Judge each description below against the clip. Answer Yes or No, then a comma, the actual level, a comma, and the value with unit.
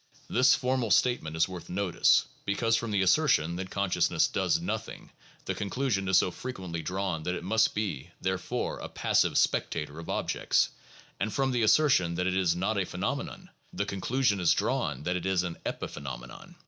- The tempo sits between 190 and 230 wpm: No, average, 180 wpm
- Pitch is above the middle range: No, very low, 95 Hz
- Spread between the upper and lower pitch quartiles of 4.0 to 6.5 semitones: Yes, average, 4.4 semitones